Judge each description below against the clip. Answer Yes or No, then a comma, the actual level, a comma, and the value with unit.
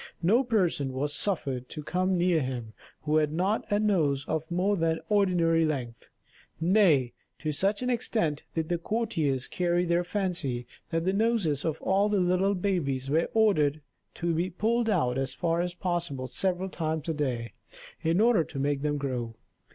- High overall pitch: No, medium, 165 Hz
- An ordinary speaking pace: Yes, average, 175 wpm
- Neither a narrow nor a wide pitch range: Yes, average, 4.8 semitones